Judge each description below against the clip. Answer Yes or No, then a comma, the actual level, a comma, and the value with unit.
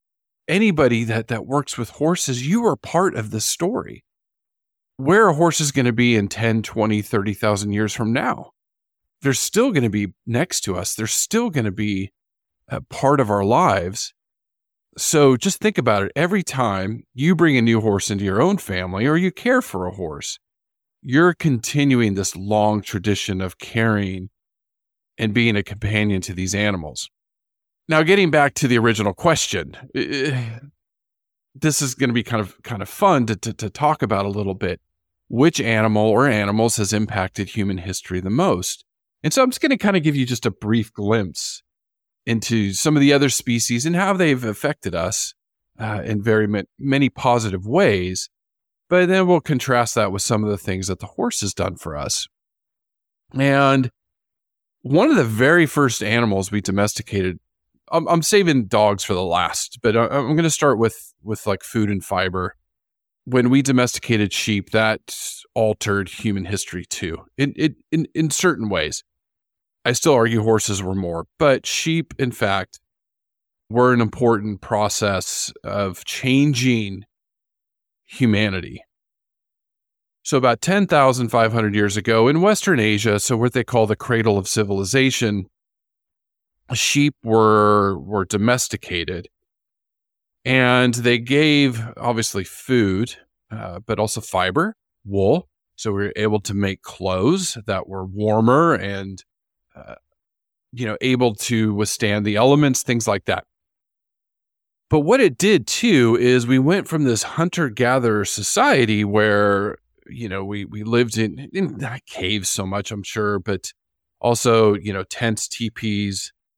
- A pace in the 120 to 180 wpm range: Yes, average, 160 wpm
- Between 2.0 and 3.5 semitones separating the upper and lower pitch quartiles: No, average, 4.8 semitones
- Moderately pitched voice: No, low, 110 Hz